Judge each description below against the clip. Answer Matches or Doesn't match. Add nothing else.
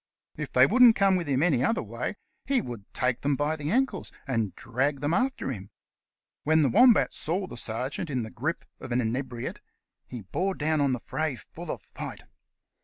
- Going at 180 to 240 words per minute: Matches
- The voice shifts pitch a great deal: Matches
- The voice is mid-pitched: Matches